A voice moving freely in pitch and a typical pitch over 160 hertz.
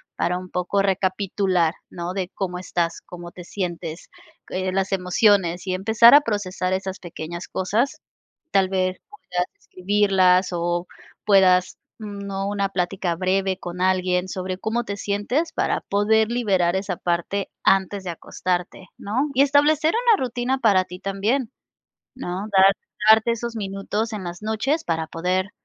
No: average, 2.7 semitones; high, 190 Hz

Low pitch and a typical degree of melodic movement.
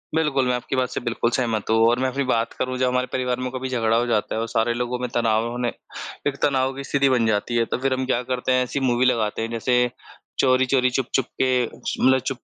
No: low, 125 Hz; narrow, 1.7 semitones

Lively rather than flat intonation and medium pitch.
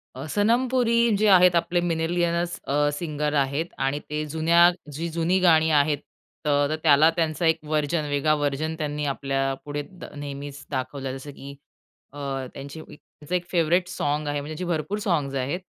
No: average, 3.1 semitones; medium, 155 Hz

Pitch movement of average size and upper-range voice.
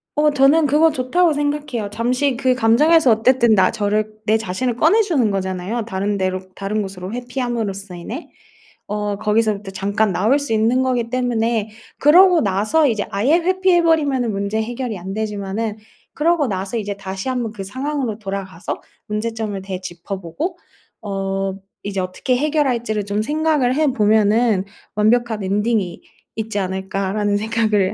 Yes: average, 4.5 semitones; high, 220 Hz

